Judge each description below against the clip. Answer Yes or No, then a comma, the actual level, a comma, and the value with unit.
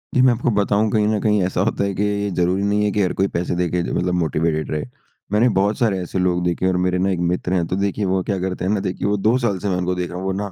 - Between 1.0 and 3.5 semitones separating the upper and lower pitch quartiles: Yes, narrow, 2.4 semitones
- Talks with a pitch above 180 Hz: No, very low, 95 Hz